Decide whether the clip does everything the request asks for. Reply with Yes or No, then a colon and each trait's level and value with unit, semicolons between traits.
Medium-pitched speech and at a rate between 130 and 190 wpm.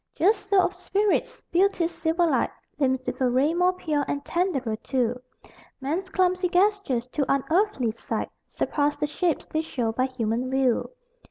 No: very high, 310 Hz; average, 160 wpm